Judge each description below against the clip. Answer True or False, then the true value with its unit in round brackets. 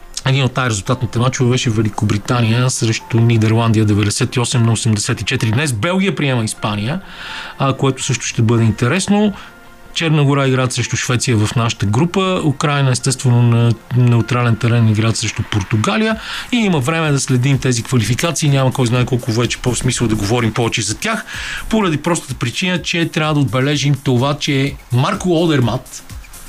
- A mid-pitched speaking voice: False (125 Hz)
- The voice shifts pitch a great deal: False (3.6 semitones)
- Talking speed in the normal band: True (150 wpm)